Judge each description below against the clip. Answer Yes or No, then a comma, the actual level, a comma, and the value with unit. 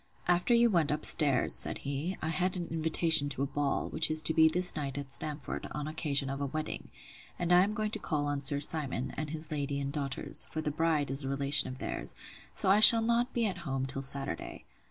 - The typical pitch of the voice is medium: Yes, medium, 155 Hz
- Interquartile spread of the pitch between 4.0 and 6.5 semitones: No, average, 3.6 semitones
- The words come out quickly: Yes, fast, 235 wpm